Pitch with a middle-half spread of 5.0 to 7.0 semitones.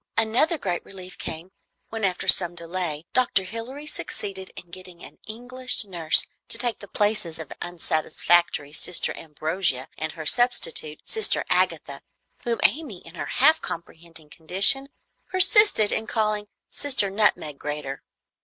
Yes: wide, 5.5 semitones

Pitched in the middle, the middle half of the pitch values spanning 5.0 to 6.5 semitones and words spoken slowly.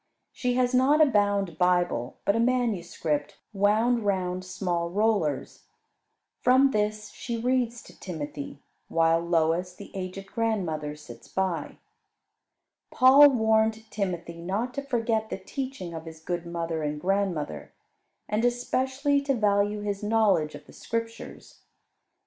No: high, 200 Hz; wide, 5.4 semitones; slow, 130 wpm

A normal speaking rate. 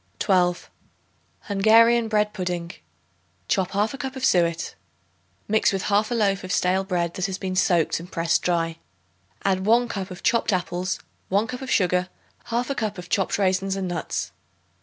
Yes: average, 160 wpm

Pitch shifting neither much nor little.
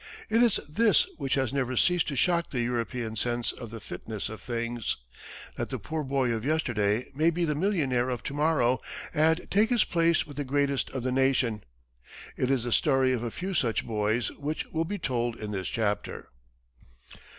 Yes: average, 5.0 semitones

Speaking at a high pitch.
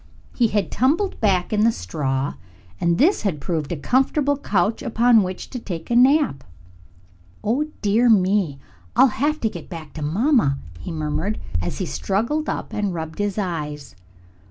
Yes: high, 205 Hz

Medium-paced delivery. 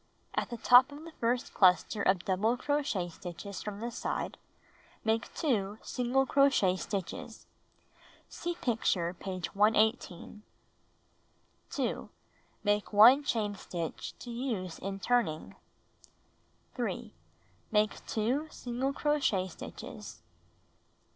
No: slow, 110 wpm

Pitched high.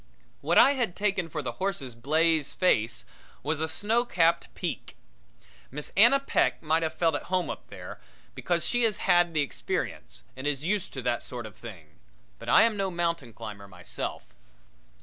No: medium, 165 Hz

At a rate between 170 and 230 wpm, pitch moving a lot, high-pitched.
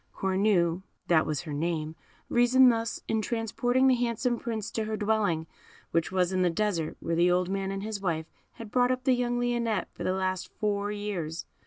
No: average, 195 wpm; average, 4.9 semitones; high, 205 Hz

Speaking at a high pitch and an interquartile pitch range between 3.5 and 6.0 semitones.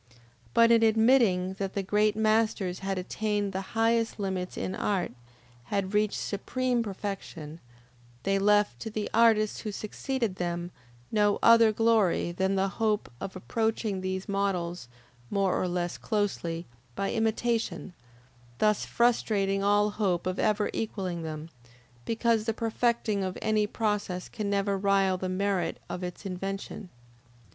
No: high, 200 Hz; average, 2.7 semitones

